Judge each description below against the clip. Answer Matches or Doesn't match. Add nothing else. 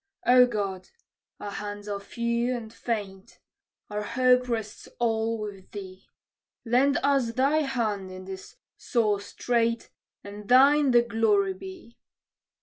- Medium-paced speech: Doesn't match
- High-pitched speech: Matches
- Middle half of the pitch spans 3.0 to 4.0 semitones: Matches